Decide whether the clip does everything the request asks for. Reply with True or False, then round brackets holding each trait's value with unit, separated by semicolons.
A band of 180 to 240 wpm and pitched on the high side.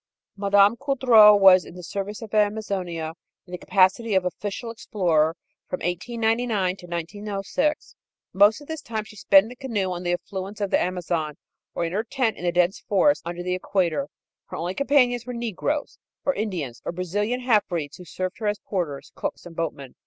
True (185 wpm; 195 Hz)